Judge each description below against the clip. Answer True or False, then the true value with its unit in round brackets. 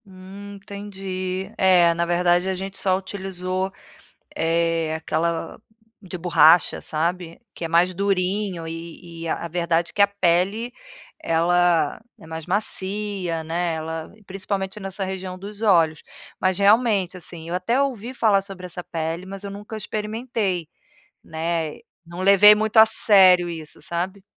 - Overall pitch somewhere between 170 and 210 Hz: True (185 Hz)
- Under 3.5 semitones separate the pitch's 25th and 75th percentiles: True (2.9 semitones)